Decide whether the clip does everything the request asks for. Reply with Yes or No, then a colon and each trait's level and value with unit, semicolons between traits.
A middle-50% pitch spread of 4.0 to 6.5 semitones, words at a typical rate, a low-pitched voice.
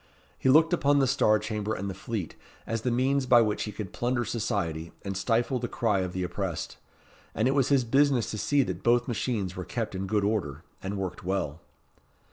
No: average, 4.6 semitones; fast, 210 wpm; low, 110 Hz